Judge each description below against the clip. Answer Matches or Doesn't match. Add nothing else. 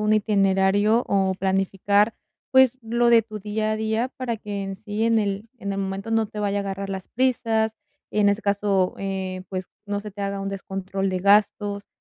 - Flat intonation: Matches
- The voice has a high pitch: Matches